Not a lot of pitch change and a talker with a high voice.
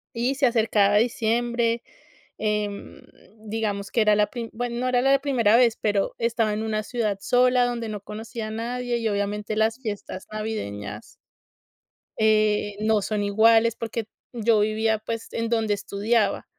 Yes: narrow, 2.0 semitones; high, 220 Hz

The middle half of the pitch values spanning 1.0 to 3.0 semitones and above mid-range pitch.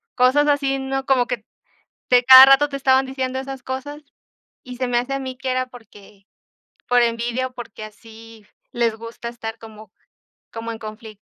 Yes: average, 2.7 semitones; very high, 250 Hz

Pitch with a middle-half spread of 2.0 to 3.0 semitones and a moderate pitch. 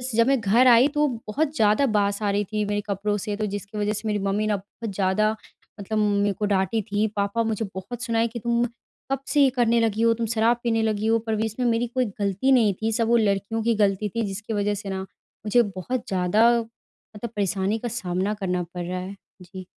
No: narrow, 2.4 semitones; high, 215 Hz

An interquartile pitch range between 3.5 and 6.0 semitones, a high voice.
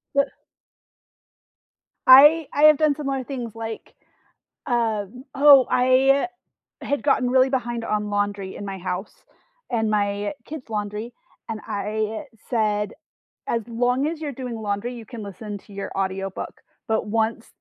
Yes: average, 4.0 semitones; high, 230 Hz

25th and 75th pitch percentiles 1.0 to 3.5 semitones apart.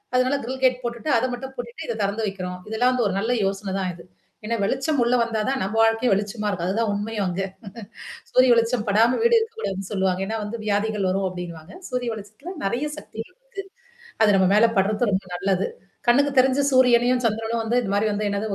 No: average, 4.0 semitones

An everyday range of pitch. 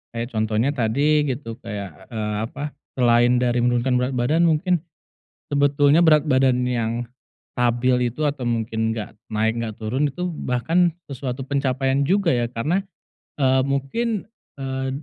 Yes: average, 3.4 semitones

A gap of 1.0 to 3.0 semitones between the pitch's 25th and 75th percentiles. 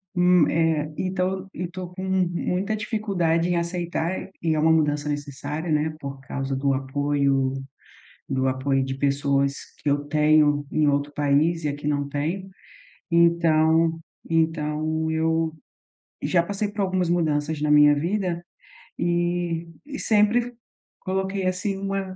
No: average, 3.7 semitones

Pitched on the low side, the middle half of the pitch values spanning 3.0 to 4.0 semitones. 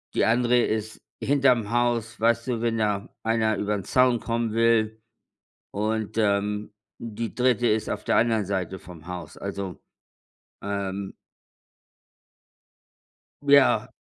No: low, 110 Hz; narrow, 2.5 semitones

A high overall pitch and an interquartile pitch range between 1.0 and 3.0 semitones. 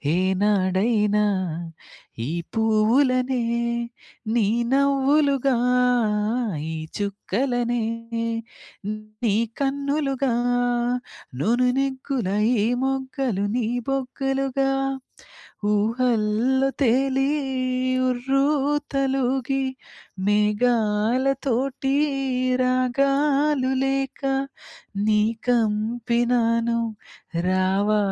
No: very high, 250 Hz; average, 3.7 semitones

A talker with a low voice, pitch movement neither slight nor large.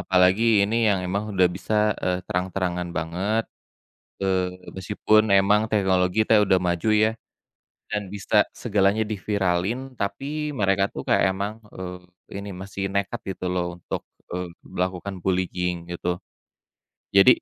No: very low, 95 Hz; narrow, 2.1 semitones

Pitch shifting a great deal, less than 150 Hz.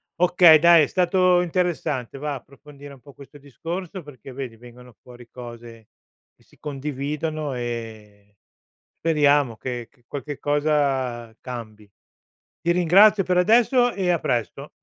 Yes: wide, 5.7 semitones; medium, 140 Hz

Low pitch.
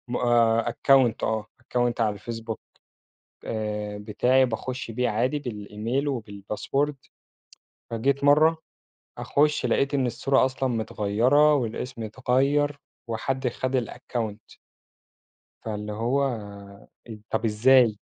Yes: low, 120 Hz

